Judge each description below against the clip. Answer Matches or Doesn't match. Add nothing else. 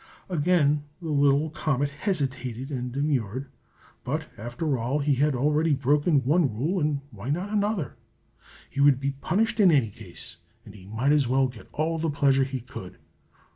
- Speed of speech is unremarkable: Matches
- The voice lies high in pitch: Doesn't match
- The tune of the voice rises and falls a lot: Doesn't match